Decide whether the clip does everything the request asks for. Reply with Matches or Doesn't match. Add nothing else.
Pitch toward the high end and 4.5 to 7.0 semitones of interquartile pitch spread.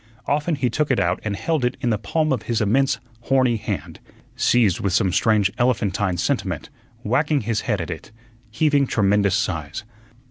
Doesn't match